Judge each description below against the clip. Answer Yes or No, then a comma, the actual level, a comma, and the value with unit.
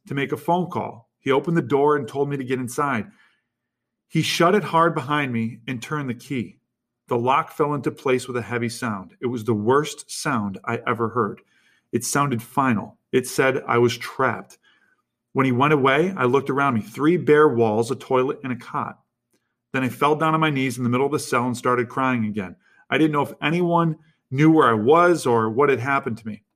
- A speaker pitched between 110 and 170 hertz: Yes, low, 135 Hz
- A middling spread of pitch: Yes, average, 3.8 semitones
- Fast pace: Yes, fast, 220 wpm